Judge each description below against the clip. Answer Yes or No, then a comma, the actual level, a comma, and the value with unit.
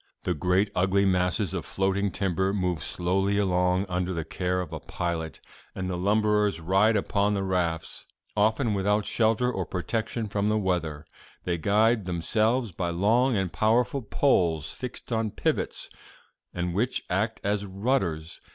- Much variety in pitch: No, average, 3.1 semitones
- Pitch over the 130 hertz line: No, very low, 95 Hz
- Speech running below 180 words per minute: Yes, average, 150 wpm